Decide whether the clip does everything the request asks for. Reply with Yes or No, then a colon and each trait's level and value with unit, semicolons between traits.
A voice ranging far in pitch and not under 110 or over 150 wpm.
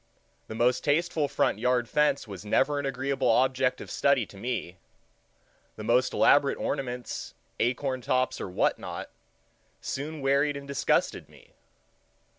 No: narrow, 2.4 semitones; average, 140 wpm